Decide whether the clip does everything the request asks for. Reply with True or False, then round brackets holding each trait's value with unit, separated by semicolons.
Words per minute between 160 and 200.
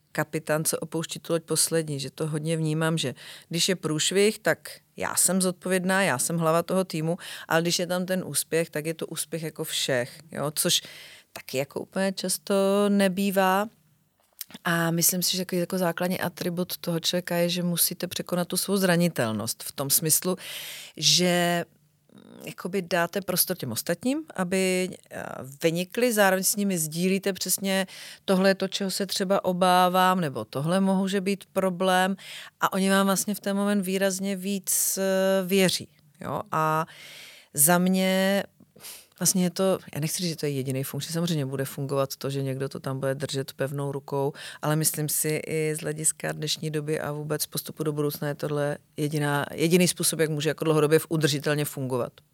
True (170 wpm)